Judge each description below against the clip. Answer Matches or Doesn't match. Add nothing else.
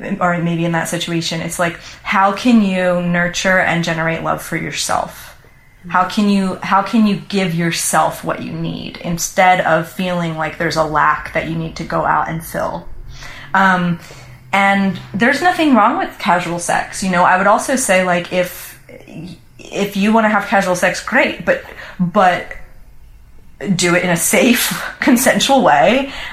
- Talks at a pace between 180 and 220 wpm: Doesn't match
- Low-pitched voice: Doesn't match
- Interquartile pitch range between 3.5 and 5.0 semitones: Doesn't match